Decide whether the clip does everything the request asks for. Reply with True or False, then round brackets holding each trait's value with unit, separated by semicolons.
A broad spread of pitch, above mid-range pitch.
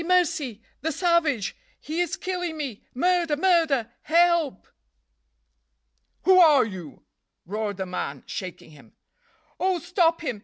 True (7.9 semitones; 315 Hz)